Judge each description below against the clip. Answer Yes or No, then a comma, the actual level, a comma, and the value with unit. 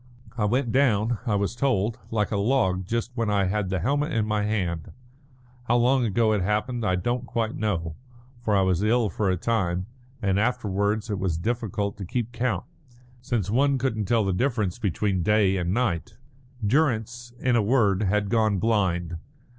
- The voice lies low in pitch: Yes, low, 105 Hz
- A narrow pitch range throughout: No, average, 3.6 semitones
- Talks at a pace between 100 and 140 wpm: No, average, 180 wpm